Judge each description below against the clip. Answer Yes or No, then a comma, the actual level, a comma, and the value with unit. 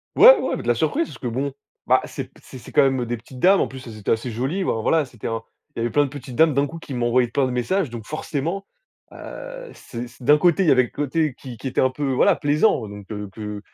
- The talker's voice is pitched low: Yes, low, 130 Hz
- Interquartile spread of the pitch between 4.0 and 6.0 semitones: Yes, average, 4.3 semitones